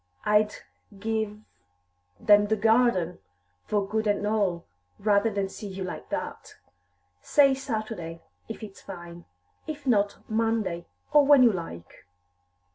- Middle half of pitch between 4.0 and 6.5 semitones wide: No, average, 2.7 semitones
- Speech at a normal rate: No, slow, 125 wpm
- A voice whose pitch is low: No, high, 210 Hz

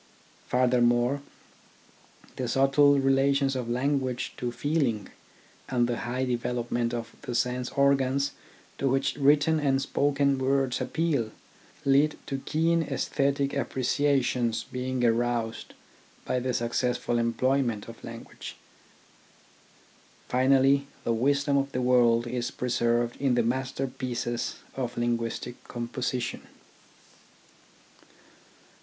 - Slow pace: Yes, slow, 105 wpm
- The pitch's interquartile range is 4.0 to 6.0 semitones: No, narrow, 2.4 semitones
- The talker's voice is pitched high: No, low, 130 Hz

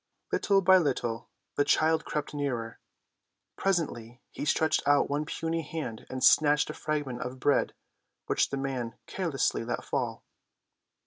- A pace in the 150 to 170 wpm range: No, average, 140 wpm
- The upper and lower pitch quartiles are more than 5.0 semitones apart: No, average, 4.1 semitones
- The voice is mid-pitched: Yes, medium, 145 Hz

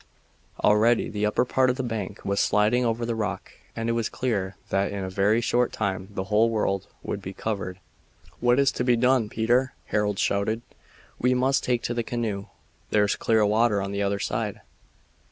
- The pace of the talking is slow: No, average, 190 wpm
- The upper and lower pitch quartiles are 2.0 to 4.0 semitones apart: Yes, average, 3.1 semitones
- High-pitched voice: No, low, 110 Hz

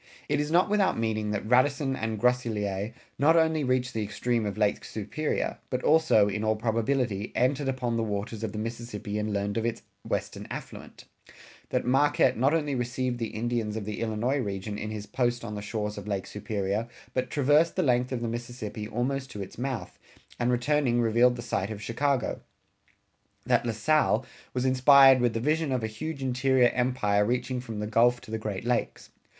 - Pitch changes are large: No, average, 3.4 semitones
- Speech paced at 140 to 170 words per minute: No, average, 190 wpm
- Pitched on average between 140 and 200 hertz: No, low, 120 Hz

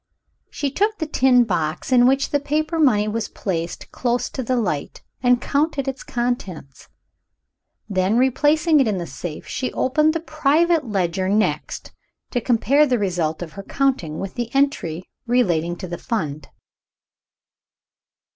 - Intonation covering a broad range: Yes, wide, 7.2 semitones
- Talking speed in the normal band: Yes, average, 150 wpm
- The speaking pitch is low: No, high, 245 Hz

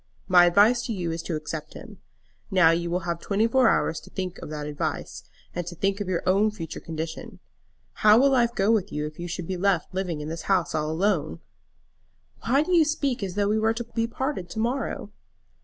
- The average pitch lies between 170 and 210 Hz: Yes, medium, 185 Hz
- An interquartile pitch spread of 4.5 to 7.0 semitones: Yes, average, 5.0 semitones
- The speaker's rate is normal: No, fast, 225 wpm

